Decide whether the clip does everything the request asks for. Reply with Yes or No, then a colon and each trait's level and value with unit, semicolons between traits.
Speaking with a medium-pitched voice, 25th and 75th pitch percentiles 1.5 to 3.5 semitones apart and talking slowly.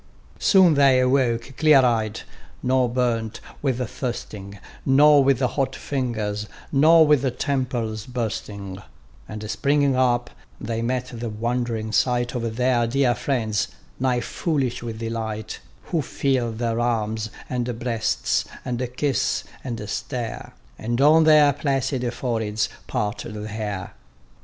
No: low, 120 Hz; average, 3.1 semitones; slow, 125 wpm